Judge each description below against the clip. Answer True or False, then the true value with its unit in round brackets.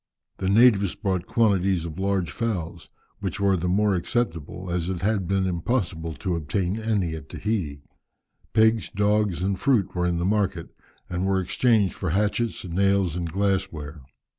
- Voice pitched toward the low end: True (95 Hz)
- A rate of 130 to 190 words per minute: True (165 wpm)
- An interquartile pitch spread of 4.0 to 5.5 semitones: False (3.1 semitones)